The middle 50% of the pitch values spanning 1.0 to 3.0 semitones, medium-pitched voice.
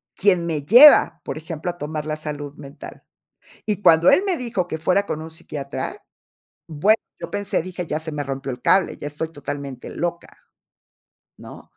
No: average, 3.9 semitones; medium, 160 Hz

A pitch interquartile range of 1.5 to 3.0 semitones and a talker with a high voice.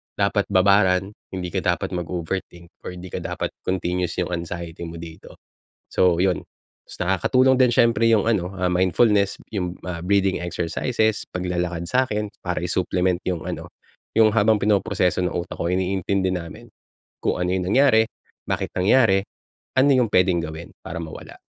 No: narrow, 2.6 semitones; very low, 95 Hz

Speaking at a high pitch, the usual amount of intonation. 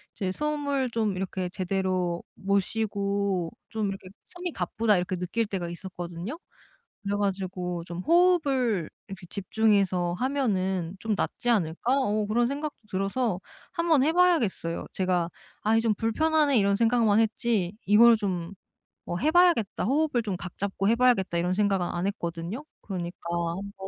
Yes: high, 200 Hz; average, 4.4 semitones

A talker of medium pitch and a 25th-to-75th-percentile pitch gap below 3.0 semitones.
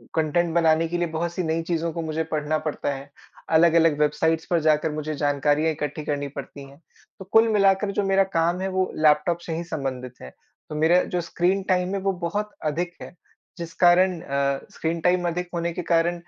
Yes: medium, 165 Hz; narrow, 2.6 semitones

